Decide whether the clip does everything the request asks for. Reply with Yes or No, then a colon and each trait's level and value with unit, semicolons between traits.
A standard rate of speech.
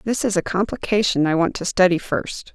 No: fast, 210 wpm